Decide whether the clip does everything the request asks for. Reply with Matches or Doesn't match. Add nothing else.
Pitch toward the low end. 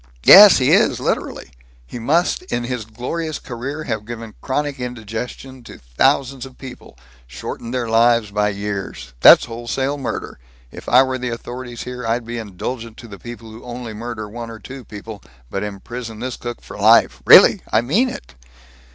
Matches